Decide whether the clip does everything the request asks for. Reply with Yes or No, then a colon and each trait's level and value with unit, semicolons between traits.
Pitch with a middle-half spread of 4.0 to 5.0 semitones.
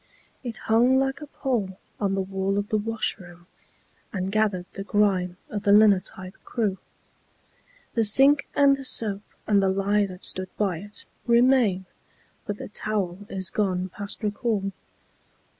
No: average, 2.8 semitones